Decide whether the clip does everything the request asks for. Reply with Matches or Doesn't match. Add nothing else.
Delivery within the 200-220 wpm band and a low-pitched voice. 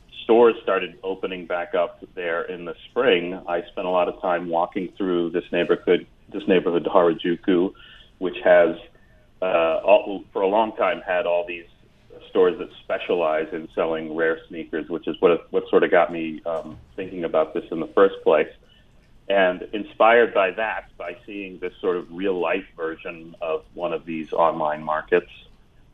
Doesn't match